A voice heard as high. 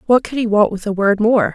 Yes: high, 215 Hz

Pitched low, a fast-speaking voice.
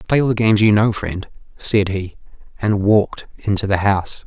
No: low, 105 Hz; average, 195 wpm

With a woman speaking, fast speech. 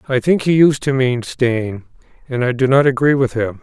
No: male; fast, 230 wpm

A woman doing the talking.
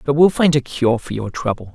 No: male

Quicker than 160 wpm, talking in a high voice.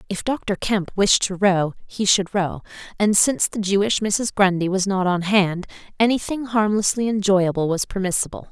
Yes: average, 170 wpm; high, 200 Hz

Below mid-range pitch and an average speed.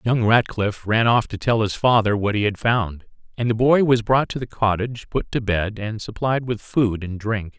No: low, 110 Hz; fast, 230 wpm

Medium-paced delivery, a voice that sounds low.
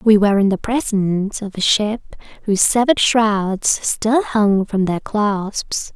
No: average, 160 wpm; high, 205 Hz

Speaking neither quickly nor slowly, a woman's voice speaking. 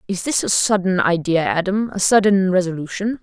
Yes: average, 165 wpm; female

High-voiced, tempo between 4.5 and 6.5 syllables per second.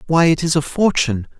No: medium, 155 Hz; 6.2 syllables/s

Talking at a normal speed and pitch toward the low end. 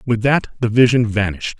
Yes: average, 190 wpm; low, 115 Hz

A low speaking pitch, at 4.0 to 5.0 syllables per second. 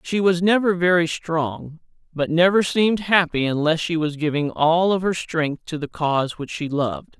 No: medium, 165 Hz; 4.7 syllables/s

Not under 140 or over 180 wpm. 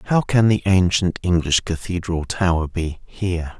Yes: average, 150 wpm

